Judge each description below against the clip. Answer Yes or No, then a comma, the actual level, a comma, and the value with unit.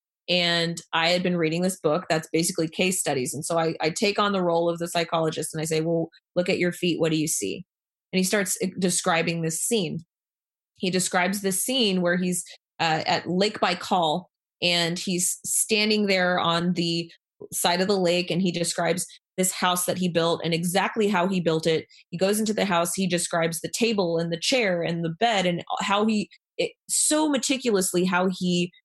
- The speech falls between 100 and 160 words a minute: No, fast, 205 wpm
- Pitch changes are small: Yes, narrow, 2.3 semitones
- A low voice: No, medium, 175 Hz